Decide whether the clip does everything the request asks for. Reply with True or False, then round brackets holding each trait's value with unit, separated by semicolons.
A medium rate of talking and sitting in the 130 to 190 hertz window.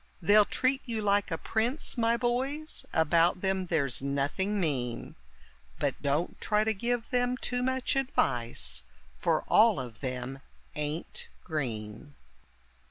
False (130 wpm; 185 Hz)